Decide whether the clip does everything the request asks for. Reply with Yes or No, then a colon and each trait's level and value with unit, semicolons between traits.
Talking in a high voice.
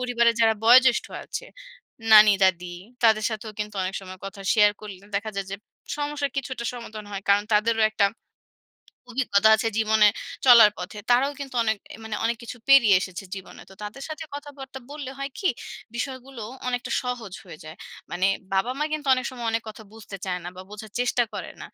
Yes: high, 220 Hz